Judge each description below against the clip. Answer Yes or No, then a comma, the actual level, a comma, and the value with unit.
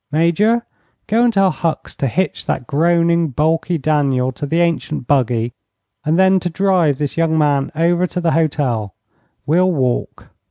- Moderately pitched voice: Yes, medium, 160 Hz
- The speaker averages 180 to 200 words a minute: No, average, 160 wpm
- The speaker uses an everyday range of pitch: Yes, average, 3.7 semitones